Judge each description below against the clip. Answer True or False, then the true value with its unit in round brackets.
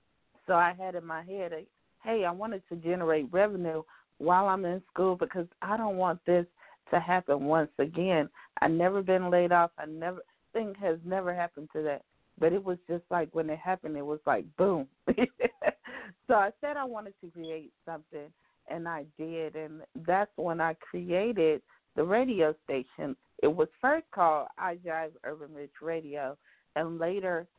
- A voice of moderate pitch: True (175 Hz)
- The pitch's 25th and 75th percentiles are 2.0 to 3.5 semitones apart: True (3.0 semitones)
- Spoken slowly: False (175 wpm)